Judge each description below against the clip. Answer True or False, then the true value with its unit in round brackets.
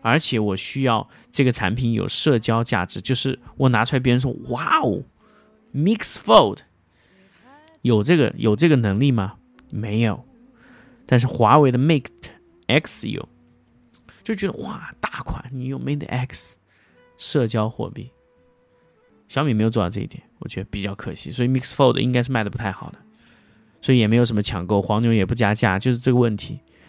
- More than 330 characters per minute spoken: False (280 characters per minute)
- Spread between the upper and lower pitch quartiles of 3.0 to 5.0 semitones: True (4.2 semitones)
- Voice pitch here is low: True (120 Hz)